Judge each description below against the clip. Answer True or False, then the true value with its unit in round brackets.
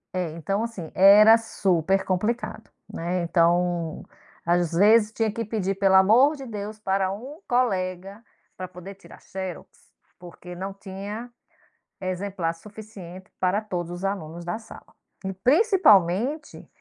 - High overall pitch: True (195 Hz)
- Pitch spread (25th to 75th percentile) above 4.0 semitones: False (3.4 semitones)